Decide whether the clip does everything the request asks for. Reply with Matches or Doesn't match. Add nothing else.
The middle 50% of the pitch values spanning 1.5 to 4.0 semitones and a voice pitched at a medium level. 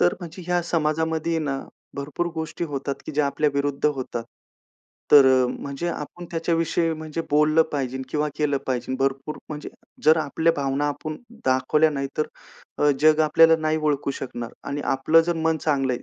Matches